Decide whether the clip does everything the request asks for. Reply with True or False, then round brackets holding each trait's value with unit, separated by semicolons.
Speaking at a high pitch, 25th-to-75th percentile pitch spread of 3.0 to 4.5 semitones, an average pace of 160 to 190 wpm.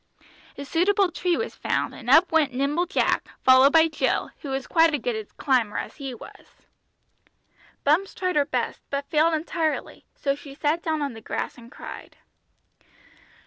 True (295 Hz; 3.5 semitones; 175 wpm)